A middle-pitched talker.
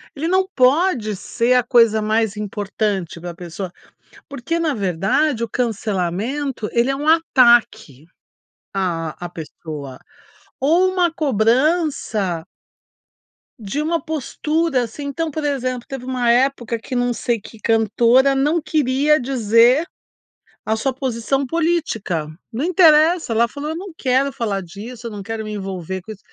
No: high, 245 Hz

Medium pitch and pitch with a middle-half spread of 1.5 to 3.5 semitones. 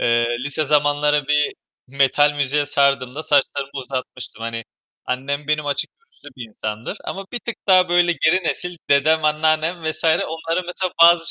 Yes: medium, 150 Hz; average, 3.0 semitones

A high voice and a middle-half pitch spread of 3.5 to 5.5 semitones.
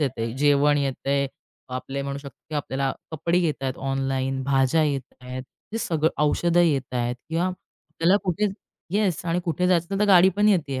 No: medium, 145 Hz; average, 4.4 semitones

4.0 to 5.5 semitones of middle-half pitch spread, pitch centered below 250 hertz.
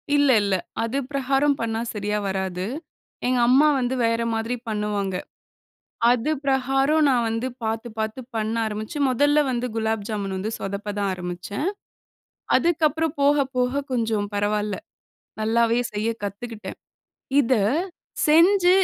Yes: average, 4.4 semitones; high, 230 Hz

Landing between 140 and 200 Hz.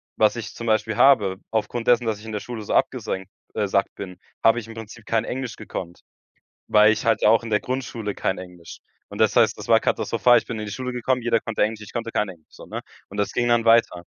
No: low, 110 Hz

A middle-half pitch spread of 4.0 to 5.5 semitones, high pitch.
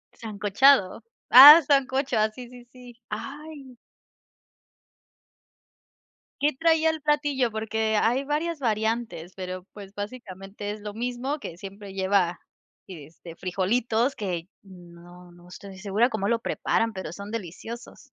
Yes: average, 4.9 semitones; high, 220 Hz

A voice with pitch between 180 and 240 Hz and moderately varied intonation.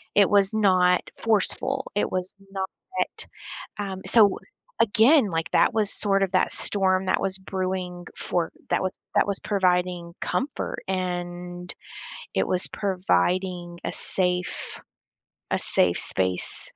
No: medium, 185 Hz; narrow, 1.9 semitones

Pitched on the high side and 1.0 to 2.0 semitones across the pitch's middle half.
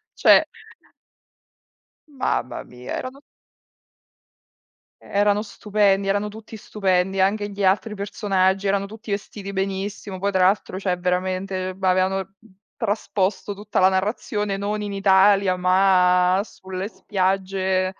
Yes: high, 195 Hz; narrow, 1.5 semitones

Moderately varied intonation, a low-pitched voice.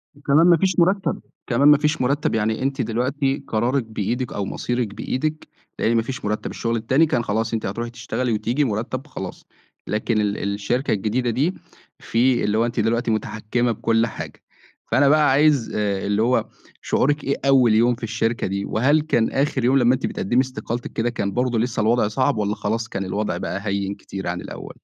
Yes: average, 3.7 semitones; low, 120 Hz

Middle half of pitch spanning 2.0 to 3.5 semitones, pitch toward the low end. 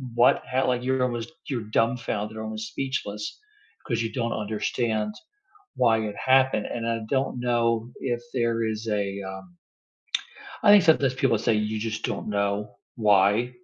Yes: average, 2.8 semitones; low, 115 Hz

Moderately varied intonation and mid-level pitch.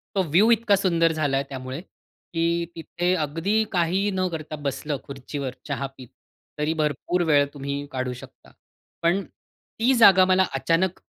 Yes: average, 4.7 semitones; medium, 165 Hz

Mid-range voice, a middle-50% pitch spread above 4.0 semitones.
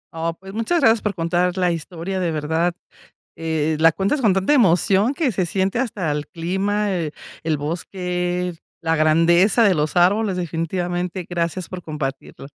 No: medium, 180 Hz; average, 2.8 semitones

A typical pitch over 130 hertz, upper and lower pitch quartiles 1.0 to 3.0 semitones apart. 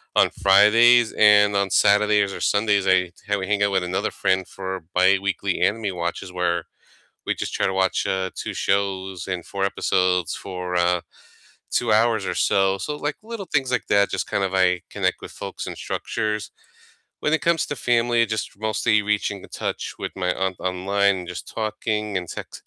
No: low, 100 Hz; narrow, 2.4 semitones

